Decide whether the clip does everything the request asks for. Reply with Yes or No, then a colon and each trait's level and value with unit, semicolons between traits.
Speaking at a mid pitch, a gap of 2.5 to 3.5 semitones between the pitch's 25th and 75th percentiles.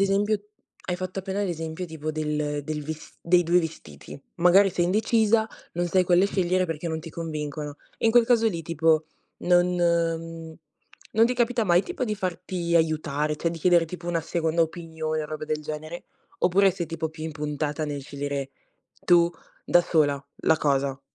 Yes: medium, 165 Hz; average, 2.8 semitones